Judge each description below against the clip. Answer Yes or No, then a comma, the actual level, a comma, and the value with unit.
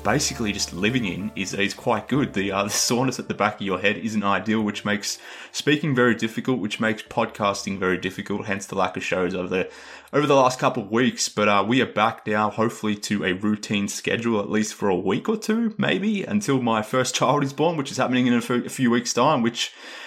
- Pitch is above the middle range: No, low, 110 Hz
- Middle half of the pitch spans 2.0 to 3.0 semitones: No, average, 4.0 semitones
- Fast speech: Yes, fast, 235 wpm